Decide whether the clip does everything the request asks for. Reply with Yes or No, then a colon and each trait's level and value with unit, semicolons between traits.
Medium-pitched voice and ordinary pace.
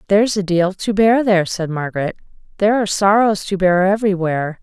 No: high, 195 Hz; average, 180 wpm